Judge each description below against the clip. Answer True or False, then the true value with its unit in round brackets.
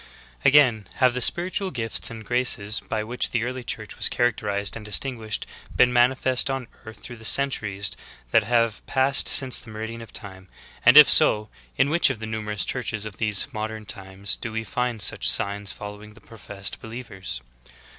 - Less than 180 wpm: False (185 wpm)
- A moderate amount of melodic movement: True (3.0 semitones)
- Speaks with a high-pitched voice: False (110 Hz)